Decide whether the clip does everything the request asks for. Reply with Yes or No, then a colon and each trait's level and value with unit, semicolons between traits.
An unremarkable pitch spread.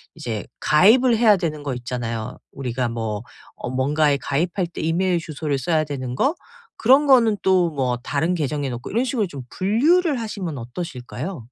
No: wide, 7.3 semitones